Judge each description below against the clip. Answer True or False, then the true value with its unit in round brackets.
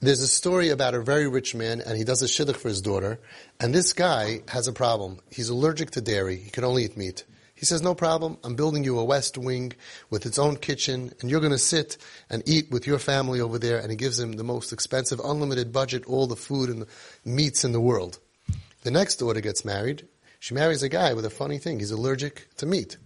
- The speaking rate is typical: False (240 wpm)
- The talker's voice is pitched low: True (125 Hz)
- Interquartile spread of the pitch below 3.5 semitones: False (3.9 semitones)